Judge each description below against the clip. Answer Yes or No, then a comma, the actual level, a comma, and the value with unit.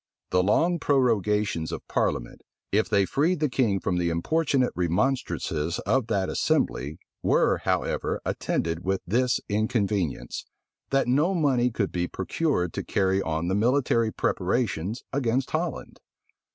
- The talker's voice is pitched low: Yes, low, 110 Hz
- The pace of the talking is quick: No, slow, 135 wpm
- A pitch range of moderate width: No, wide, 6.4 semitones